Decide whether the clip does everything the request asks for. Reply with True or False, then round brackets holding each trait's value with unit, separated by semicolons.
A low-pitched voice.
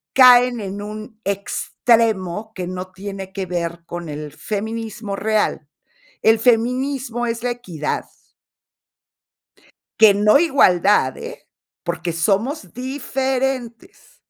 False (215 Hz)